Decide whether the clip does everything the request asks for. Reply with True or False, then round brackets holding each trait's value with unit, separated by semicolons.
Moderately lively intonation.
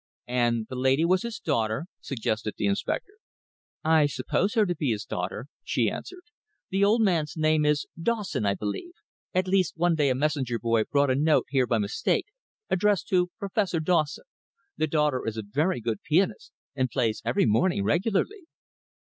False (7.6 semitones)